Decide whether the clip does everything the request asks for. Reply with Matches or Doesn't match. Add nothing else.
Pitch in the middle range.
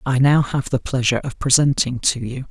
Doesn't match